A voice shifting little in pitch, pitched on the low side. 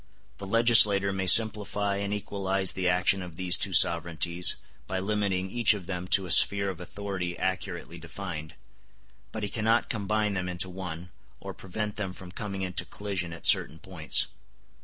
Yes: narrow, 2.2 semitones; very low, 95 Hz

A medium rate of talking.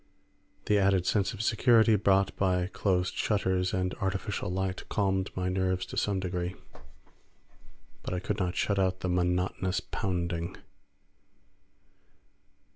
No: slow, 125 wpm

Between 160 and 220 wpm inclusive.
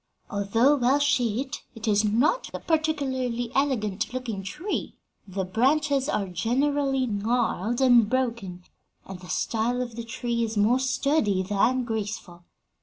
No: slow, 135 wpm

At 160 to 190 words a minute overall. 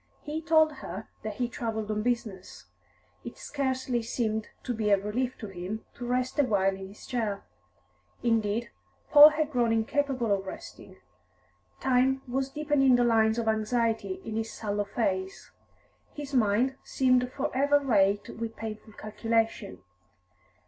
No: average, 145 wpm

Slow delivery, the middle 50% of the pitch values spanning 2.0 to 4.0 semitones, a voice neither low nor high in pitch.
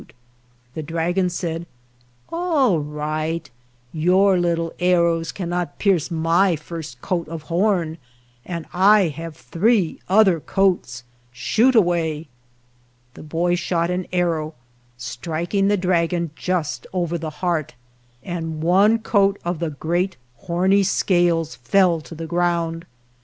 Yes: slow, 130 wpm; narrow, 2.4 semitones; medium, 170 Hz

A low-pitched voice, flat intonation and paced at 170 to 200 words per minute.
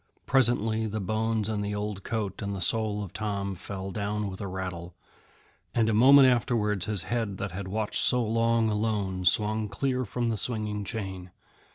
Yes: low, 105 Hz; narrow, 2.3 semitones; average, 180 wpm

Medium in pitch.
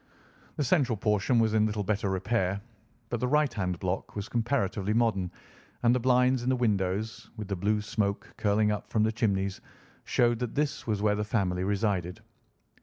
No: low, 105 Hz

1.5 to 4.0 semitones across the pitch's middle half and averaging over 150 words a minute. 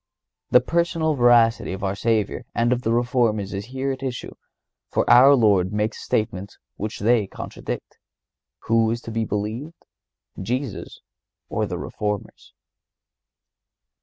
No: average, 3.1 semitones; slow, 135 wpm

